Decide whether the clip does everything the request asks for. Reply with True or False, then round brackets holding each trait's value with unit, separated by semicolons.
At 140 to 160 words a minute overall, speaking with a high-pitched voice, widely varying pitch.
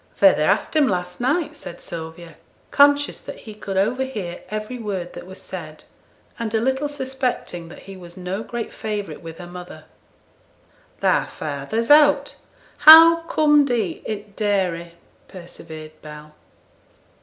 True (145 wpm; 205 Hz; 7.2 semitones)